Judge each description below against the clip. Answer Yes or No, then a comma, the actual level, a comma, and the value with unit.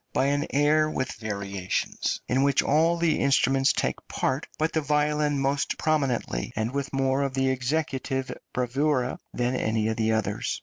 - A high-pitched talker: No, low, 135 Hz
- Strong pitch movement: No, average, 3.0 semitones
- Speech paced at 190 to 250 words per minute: No, average, 160 wpm